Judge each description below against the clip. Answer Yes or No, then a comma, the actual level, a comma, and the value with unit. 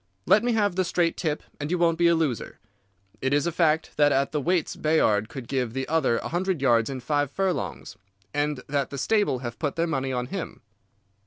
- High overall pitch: No, medium, 150 Hz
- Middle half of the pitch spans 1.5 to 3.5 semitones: No, average, 4.3 semitones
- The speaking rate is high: Yes, fast, 220 wpm